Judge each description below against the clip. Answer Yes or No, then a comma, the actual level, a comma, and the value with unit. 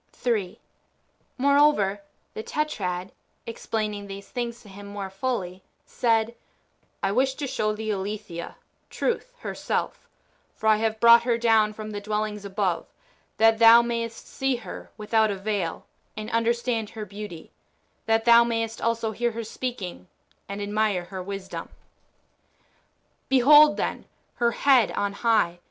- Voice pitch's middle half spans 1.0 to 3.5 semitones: Yes, narrow, 2.6 semitones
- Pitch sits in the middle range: No, high, 220 Hz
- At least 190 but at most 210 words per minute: No, average, 145 wpm